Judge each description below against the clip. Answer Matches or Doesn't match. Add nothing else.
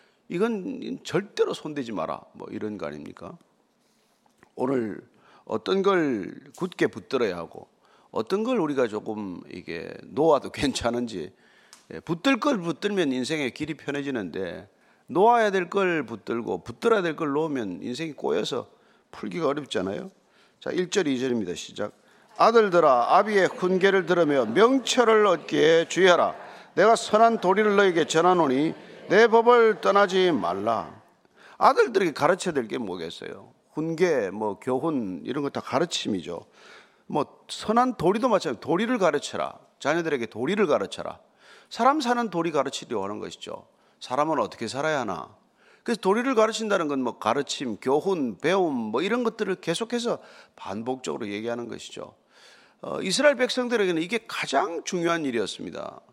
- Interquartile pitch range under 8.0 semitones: Matches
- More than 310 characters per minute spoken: Matches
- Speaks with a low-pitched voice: Doesn't match